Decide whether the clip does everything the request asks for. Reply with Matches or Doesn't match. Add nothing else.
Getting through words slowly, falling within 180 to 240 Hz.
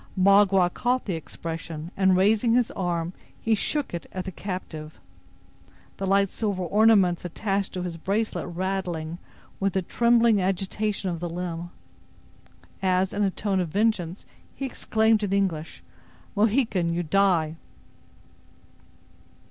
Matches